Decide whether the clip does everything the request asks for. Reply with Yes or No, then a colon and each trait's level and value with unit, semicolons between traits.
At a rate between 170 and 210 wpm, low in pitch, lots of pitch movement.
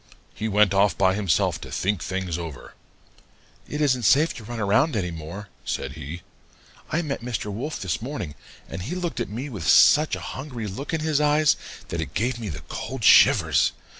Yes: average, 195 wpm; low, 105 Hz; wide, 7.4 semitones